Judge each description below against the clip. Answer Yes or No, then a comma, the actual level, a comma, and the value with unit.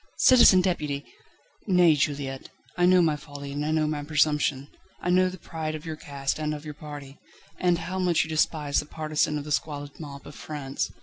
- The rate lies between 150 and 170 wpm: No, average, 200 wpm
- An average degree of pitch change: No, narrow, 2.2 semitones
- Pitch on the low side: No, medium, 150 Hz